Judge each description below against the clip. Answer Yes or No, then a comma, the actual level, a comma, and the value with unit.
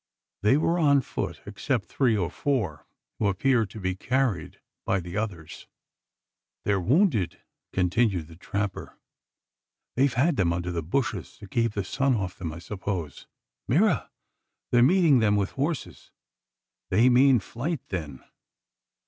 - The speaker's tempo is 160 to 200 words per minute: No, average, 145 wpm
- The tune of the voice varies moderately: No, wide, 6.2 semitones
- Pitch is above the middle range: No, low, 105 Hz